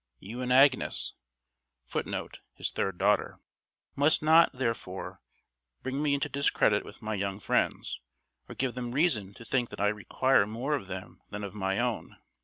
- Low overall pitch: Yes, low, 120 Hz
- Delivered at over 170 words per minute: No, average, 165 wpm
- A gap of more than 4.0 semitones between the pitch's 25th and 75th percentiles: Yes, average, 5.0 semitones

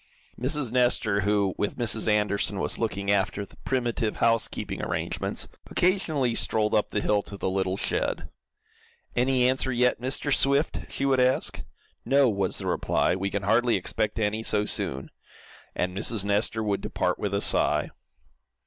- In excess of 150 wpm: Yes, average, 160 wpm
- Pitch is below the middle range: Yes, low, 110 Hz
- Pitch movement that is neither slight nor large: Yes, average, 3.9 semitones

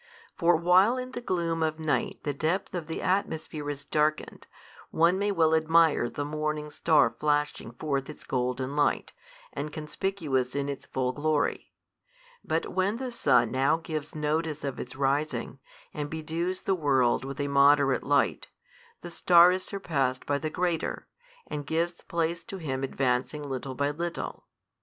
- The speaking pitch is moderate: Yes, medium, 155 Hz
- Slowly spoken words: No, average, 160 wpm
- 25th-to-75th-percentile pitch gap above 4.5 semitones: No, average, 3.1 semitones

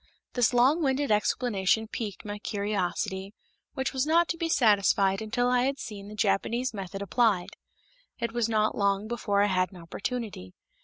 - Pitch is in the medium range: No, high, 215 Hz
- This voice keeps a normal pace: Yes, average, 165 wpm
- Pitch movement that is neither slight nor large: Yes, average, 3.8 semitones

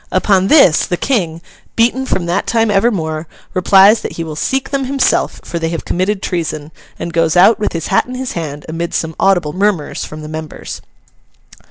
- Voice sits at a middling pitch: Yes, medium, 180 Hz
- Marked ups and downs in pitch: No, average, 4.7 semitones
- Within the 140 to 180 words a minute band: No, average, 190 wpm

